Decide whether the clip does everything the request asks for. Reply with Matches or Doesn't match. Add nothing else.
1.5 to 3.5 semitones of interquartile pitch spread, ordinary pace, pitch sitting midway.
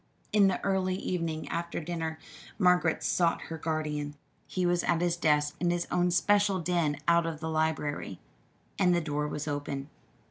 Matches